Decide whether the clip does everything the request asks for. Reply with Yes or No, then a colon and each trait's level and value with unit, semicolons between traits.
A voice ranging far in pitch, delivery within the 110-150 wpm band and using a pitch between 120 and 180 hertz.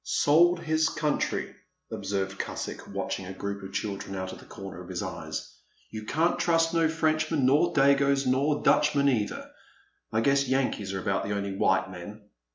No: wide, 7.5 semitones; average, 180 wpm; low, 135 Hz